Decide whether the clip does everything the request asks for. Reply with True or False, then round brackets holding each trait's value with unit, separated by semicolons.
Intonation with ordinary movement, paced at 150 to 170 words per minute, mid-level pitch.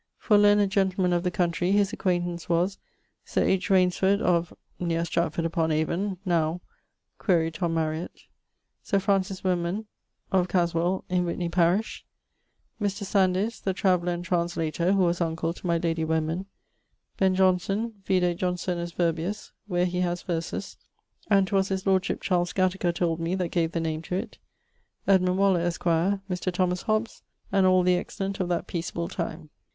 False (2.0 semitones; 160 wpm; 180 Hz)